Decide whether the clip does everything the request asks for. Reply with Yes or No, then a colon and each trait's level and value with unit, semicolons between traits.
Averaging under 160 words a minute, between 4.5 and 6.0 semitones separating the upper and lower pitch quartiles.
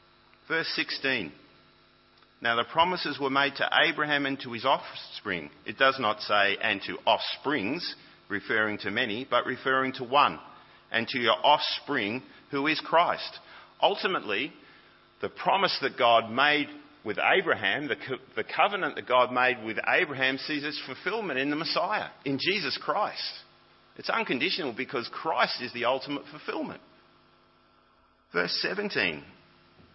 Yes: average, 140 wpm; average, 5.1 semitones